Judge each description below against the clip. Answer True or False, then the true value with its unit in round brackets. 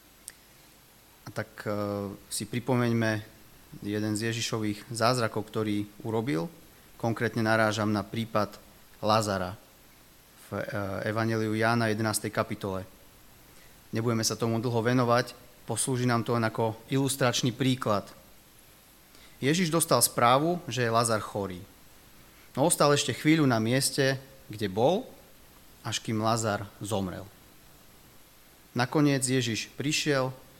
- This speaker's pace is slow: True (105 wpm)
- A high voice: False (115 Hz)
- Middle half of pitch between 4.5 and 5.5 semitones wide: False (3.2 semitones)